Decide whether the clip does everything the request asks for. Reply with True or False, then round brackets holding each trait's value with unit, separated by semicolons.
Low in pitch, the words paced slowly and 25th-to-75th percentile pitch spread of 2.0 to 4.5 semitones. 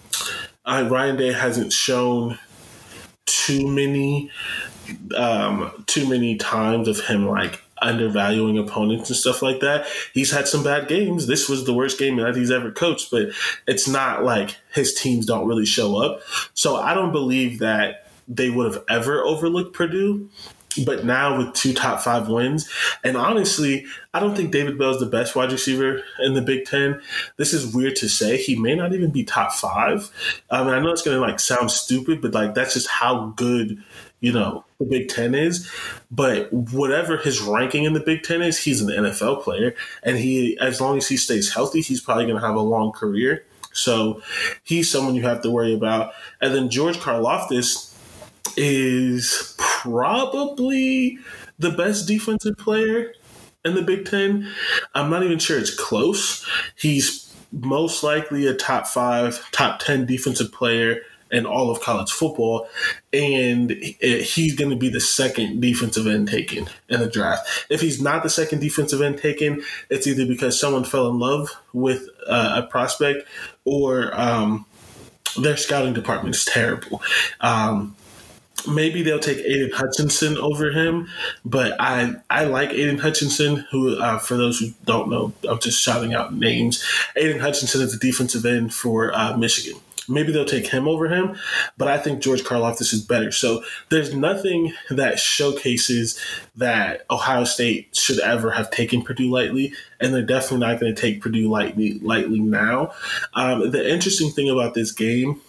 False (130 Hz; 170 wpm; 4.0 semitones)